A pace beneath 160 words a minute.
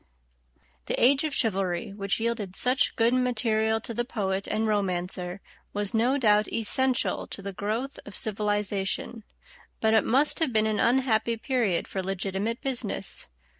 Yes: average, 150 wpm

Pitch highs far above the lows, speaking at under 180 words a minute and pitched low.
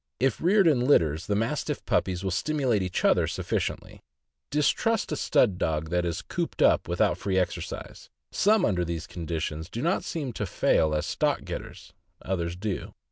Yes: wide, 8.0 semitones; average, 170 wpm; very low, 95 Hz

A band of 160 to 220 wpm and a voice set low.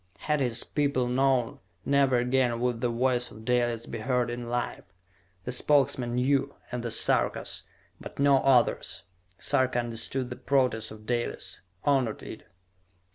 No: average, 145 wpm; low, 125 Hz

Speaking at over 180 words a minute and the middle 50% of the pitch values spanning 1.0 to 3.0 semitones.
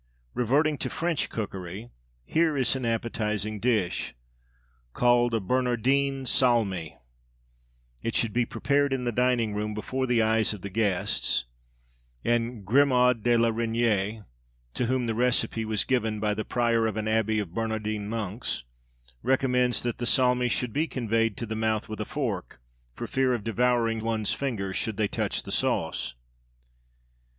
No: average, 155 wpm; narrow, 2.6 semitones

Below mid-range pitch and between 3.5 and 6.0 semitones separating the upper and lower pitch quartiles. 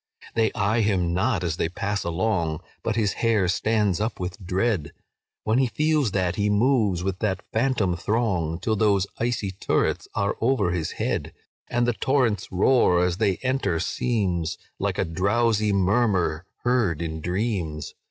Yes: low, 100 Hz; average, 4.3 semitones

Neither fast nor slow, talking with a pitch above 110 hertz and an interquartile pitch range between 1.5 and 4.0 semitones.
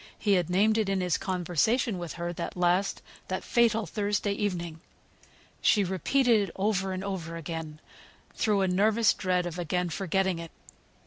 Yes: average, 165 wpm; high, 190 Hz; average, 2.8 semitones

